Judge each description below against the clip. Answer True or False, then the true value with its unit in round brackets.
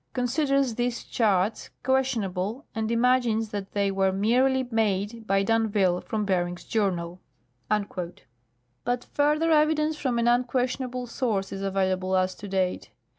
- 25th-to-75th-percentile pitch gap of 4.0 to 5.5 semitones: True (4.6 semitones)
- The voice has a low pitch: False (220 Hz)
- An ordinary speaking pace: False (125 wpm)